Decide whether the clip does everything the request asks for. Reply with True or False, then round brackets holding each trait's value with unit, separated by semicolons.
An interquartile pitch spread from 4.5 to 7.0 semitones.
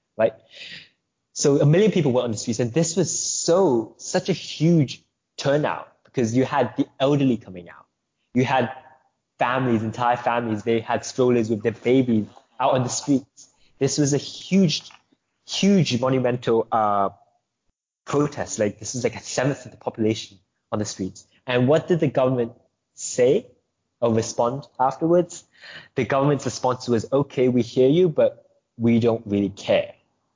False (3.8 semitones)